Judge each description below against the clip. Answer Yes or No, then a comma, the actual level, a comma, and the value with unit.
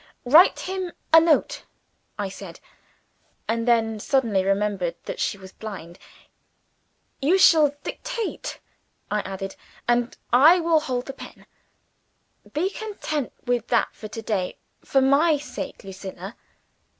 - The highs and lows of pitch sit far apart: Yes, wide, 7.6 semitones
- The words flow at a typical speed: No, slow, 125 wpm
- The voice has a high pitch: Yes, high, 245 Hz